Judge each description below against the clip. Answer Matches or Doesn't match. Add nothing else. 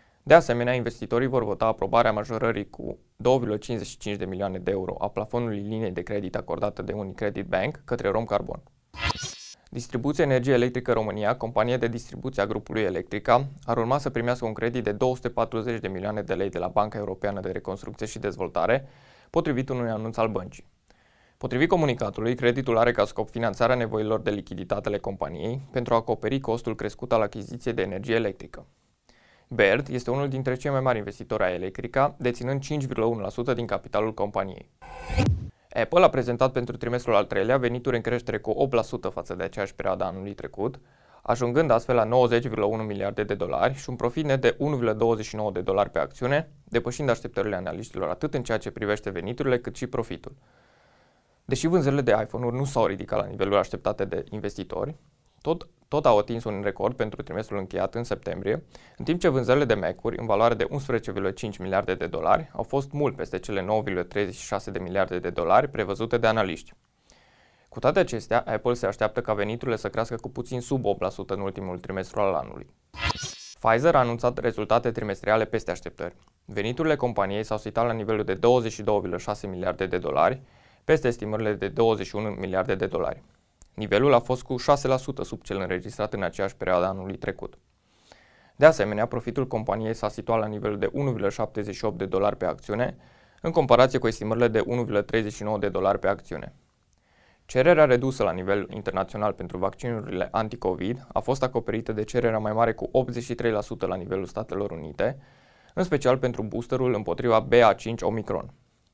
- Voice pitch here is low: Matches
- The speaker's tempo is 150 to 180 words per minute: Matches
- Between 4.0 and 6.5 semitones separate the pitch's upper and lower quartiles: Doesn't match